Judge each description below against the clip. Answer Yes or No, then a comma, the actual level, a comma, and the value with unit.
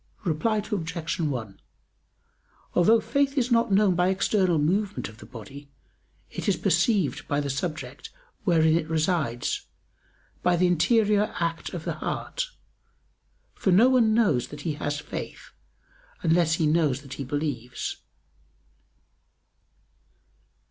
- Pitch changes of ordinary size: No, wide, 5.9 semitones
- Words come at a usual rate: No, slow, 130 wpm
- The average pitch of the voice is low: No, medium, 165 Hz